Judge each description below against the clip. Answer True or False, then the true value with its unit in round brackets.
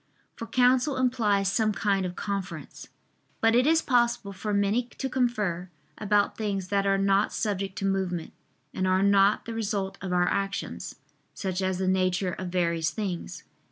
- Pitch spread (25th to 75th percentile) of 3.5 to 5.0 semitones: False (3.0 semitones)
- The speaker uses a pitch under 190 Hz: False (200 Hz)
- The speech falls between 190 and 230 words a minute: False (165 wpm)